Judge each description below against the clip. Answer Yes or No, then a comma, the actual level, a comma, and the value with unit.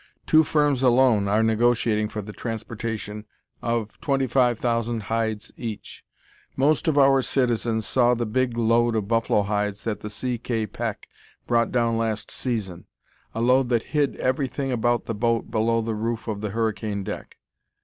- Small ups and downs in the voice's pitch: Yes, narrow, 2.3 semitones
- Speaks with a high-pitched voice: No, low, 115 Hz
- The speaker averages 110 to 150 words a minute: No, average, 165 wpm